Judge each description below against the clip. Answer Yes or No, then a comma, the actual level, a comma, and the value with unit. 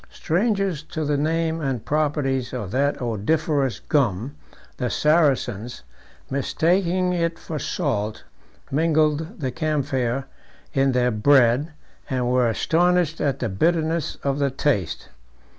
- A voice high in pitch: No, medium, 145 Hz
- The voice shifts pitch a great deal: No, average, 4.2 semitones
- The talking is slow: Yes, slow, 120 wpm